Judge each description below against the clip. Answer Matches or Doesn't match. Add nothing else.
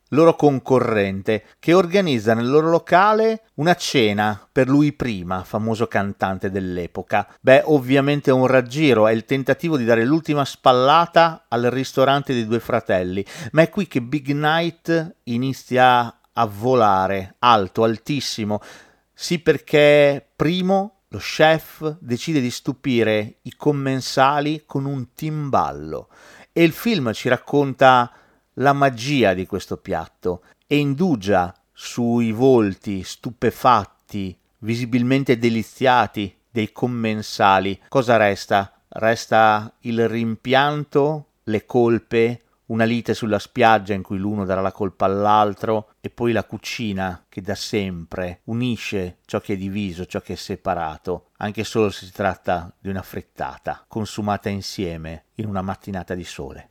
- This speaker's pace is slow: Doesn't match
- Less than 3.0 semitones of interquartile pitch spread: Doesn't match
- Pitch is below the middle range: Matches